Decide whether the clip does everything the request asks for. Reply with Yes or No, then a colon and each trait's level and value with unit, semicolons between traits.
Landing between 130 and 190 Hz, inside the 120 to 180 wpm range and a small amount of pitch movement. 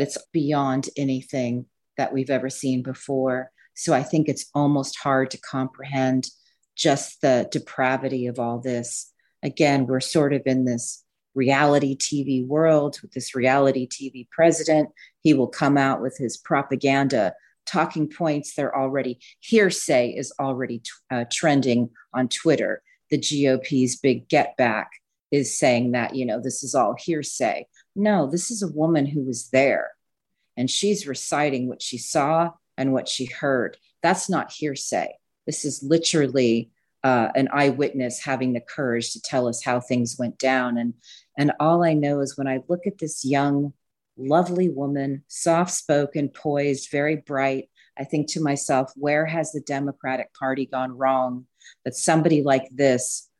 Yes: low, 135 Hz; average, 155 wpm; narrow, 2.3 semitones